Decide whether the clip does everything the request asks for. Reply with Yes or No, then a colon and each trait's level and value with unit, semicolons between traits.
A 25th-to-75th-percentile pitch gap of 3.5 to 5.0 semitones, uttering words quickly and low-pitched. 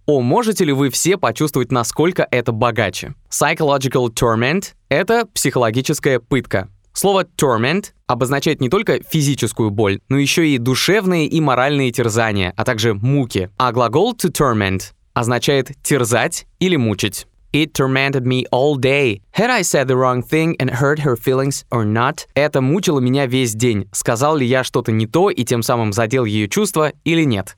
Yes: average, 4.1 semitones; fast, 165 wpm; low, 130 Hz